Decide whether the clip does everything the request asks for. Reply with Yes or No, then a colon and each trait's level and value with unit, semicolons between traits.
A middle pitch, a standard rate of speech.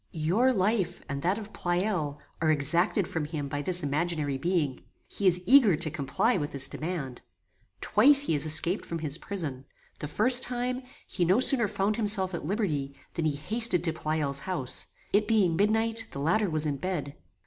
Yes: medium, 175 Hz; average, 180 wpm